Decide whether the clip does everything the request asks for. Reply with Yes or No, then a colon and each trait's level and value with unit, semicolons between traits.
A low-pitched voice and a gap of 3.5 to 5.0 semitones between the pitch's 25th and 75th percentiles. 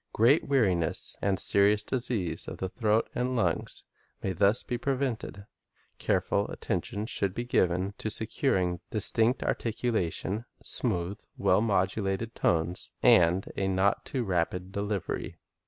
Yes: low, 100 Hz; average, 3.8 semitones